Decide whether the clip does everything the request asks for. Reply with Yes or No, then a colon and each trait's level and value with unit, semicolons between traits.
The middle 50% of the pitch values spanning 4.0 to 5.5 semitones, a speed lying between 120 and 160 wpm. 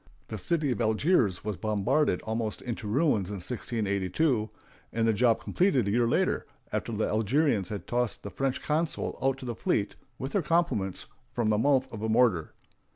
No: average, 4.3 semitones; average, 180 wpm